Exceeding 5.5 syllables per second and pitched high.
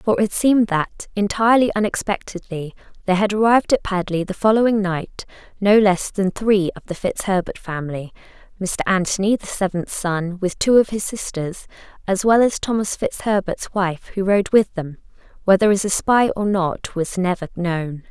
No: 4.9 syllables/s; high, 195 Hz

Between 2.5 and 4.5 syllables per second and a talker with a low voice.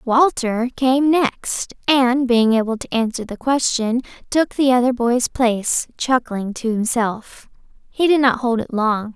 No: 4.0 syllables/s; high, 245 Hz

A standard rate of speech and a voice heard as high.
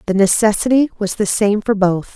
Yes: average, 195 wpm; high, 210 Hz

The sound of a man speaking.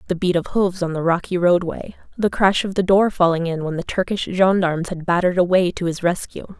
No: female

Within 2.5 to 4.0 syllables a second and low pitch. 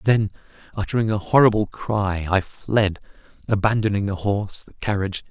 No: 5.3 syllables/s; low, 100 Hz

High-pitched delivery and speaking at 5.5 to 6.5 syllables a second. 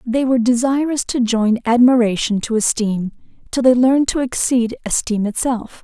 No: high, 240 Hz; 5.0 syllables/s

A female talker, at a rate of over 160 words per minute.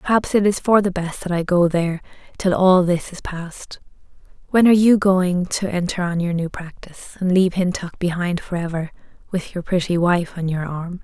Yes: female; average, 200 wpm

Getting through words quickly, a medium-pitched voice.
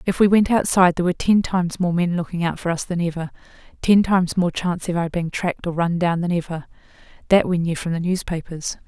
Yes: fast, 235 wpm; medium, 175 Hz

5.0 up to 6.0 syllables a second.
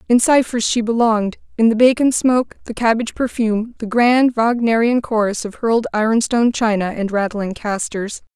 Yes: 5.4 syllables/s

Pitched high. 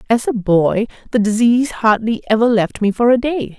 Yes: high, 225 Hz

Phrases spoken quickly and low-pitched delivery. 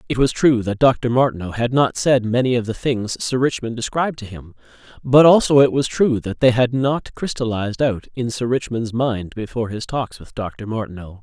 Yes: fast, 210 wpm; low, 120 Hz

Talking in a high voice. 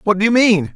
Yes: high, 210 Hz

